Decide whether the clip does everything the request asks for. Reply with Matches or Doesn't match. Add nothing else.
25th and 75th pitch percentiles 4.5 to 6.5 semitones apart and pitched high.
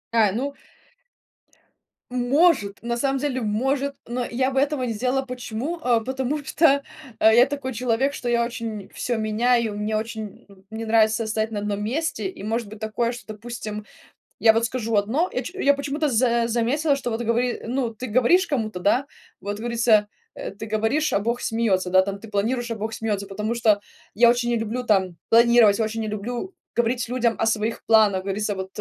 Doesn't match